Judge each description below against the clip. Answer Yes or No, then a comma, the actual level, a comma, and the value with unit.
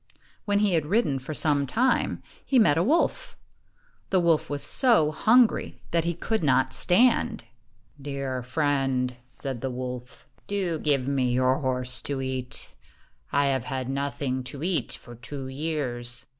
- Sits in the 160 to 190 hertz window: No, medium, 140 Hz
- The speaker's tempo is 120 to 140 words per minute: No, average, 155 wpm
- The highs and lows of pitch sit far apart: No, average, 4.7 semitones